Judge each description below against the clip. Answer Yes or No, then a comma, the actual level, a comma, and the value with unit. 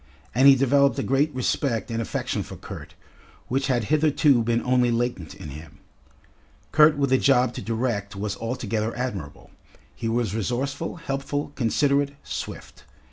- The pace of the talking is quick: No, average, 150 wpm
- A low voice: Yes, low, 125 Hz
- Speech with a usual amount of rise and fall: Yes, average, 3.6 semitones